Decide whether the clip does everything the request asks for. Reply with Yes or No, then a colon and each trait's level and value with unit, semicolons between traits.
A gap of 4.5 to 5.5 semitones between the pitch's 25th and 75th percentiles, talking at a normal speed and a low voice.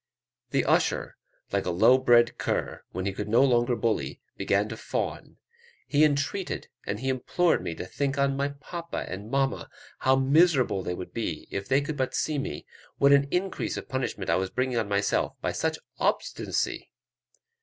Yes: average, 5.2 semitones; average, 180 wpm; low, 130 Hz